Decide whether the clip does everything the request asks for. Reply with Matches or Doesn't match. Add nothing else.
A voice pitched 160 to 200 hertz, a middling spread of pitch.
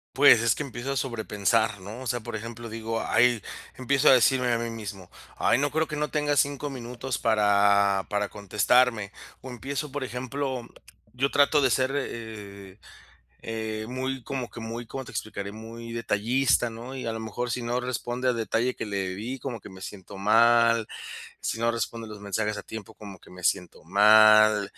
Doesn't match